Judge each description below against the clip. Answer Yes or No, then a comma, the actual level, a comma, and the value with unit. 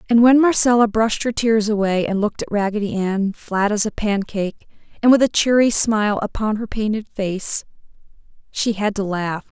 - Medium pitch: No, high, 215 Hz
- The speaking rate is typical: Yes, average, 180 wpm